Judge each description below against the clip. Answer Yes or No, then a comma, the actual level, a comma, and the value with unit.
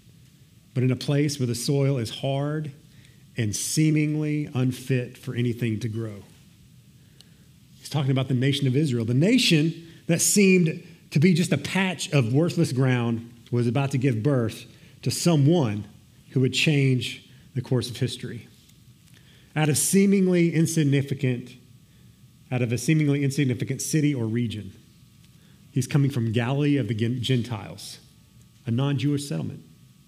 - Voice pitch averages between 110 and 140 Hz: Yes, low, 135 Hz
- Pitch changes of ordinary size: Yes, average, 3.6 semitones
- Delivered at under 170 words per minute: Yes, average, 145 wpm